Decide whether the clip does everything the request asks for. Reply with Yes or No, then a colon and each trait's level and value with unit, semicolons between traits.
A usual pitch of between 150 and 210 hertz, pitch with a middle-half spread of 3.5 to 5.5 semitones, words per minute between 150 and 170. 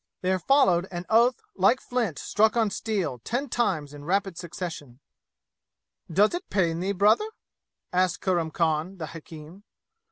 No: medium, 185 Hz; average, 4.8 semitones; average, 140 wpm